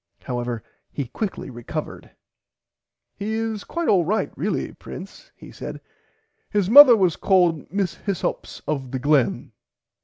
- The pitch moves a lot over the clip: Yes, wide, 7.6 semitones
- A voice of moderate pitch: Yes, medium, 180 Hz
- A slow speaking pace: Yes, slow, 125 wpm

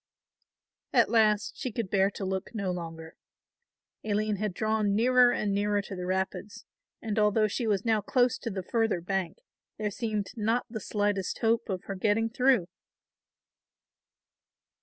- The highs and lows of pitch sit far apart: No, average, 2.7 semitones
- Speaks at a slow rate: No, average, 155 wpm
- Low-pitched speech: No, high, 210 Hz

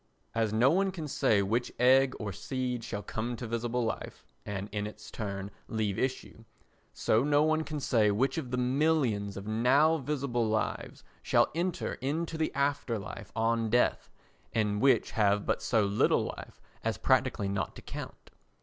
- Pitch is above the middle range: No, low, 120 Hz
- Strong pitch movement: No, average, 4.5 semitones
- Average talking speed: Yes, average, 170 wpm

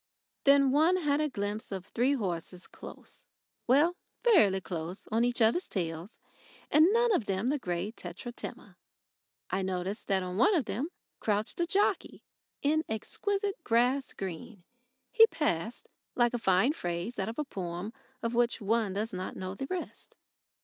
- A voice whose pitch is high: Yes, high, 230 Hz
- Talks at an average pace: Yes, average, 160 wpm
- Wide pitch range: Yes, wide, 7.3 semitones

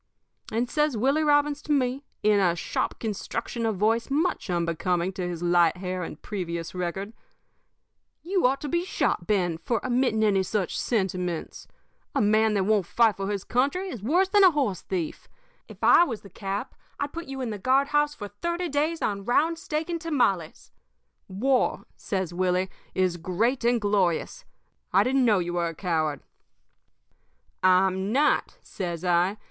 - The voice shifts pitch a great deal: Yes, wide, 7.0 semitones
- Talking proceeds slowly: No, average, 170 wpm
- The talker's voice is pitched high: Yes, high, 210 Hz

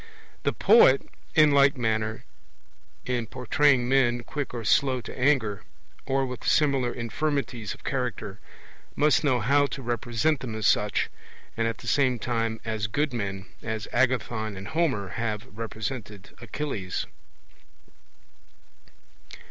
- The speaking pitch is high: No, low, 120 Hz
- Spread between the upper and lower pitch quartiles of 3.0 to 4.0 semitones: Yes, average, 3.7 semitones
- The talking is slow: Yes, slow, 130 wpm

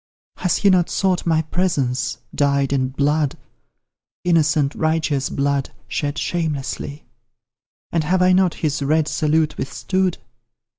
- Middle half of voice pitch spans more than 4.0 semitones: No, average, 3.6 semitones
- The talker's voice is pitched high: No, medium, 155 Hz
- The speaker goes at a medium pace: No, slow, 120 wpm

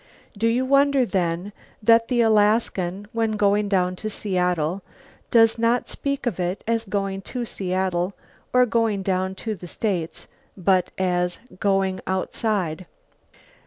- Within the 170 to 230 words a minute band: No, slow, 135 wpm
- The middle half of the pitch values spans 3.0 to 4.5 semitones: Yes, average, 3.7 semitones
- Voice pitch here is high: Yes, high, 200 Hz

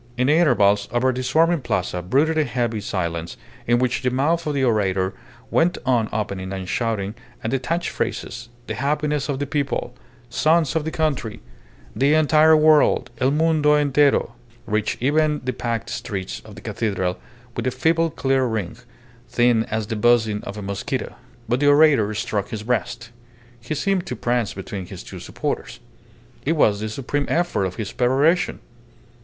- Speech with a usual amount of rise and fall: No, wide, 5.8 semitones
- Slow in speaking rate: No, average, 170 wpm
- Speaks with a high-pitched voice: No, low, 125 Hz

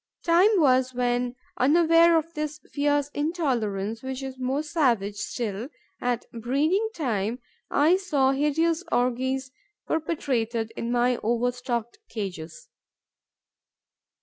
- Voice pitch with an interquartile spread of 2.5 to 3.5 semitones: No, average, 4.3 semitones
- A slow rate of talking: Yes, slow, 105 wpm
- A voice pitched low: No, very high, 260 Hz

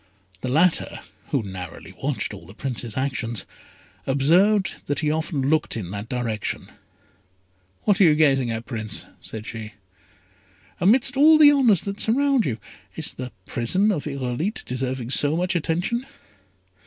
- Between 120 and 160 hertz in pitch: Yes, medium, 140 Hz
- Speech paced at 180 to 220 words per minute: No, average, 145 wpm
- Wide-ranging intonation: Yes, wide, 8.5 semitones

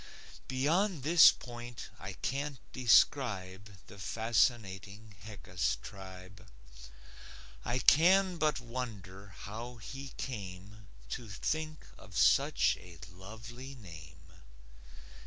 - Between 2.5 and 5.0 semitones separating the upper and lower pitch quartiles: No, wide, 5.4 semitones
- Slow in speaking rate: Yes, slow, 95 wpm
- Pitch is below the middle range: Yes, low, 110 Hz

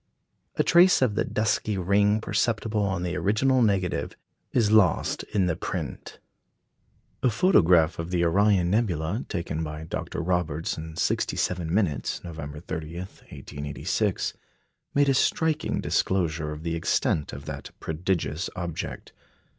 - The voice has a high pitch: No, very low, 90 Hz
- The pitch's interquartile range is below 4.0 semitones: No, average, 4.7 semitones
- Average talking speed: No, slow, 130 wpm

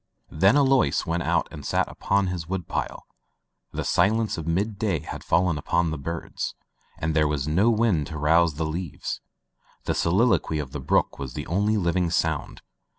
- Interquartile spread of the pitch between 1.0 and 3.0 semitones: No, average, 4.1 semitones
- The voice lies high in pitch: No, very low, 85 Hz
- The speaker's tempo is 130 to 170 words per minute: No, average, 180 wpm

